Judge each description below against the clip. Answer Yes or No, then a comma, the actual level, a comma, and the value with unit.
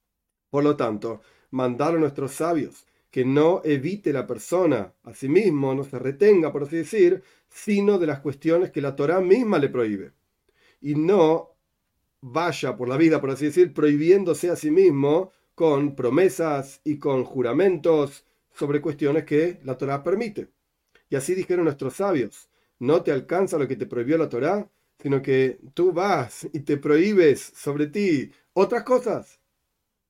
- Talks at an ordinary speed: Yes, average, 155 wpm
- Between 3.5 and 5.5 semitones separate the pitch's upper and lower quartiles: Yes, average, 4.0 semitones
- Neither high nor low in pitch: Yes, medium, 150 Hz